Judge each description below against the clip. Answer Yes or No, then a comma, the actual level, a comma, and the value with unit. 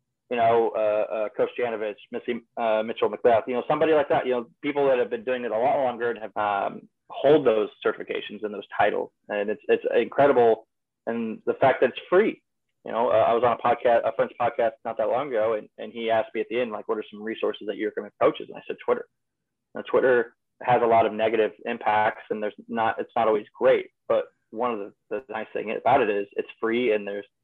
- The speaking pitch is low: Yes, low, 120 Hz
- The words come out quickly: Yes, fast, 240 wpm